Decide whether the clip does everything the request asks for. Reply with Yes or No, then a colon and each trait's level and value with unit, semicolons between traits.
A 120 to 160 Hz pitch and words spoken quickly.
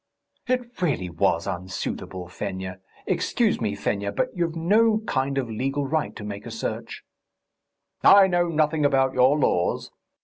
No: low, 135 Hz; average, 145 wpm